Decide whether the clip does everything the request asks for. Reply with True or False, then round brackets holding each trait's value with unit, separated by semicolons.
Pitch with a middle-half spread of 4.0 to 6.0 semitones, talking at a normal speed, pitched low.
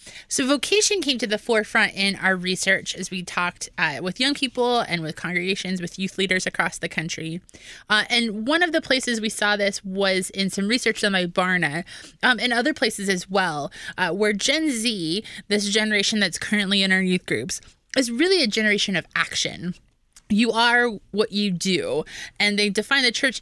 False (4.3 semitones; 190 wpm; 205 Hz)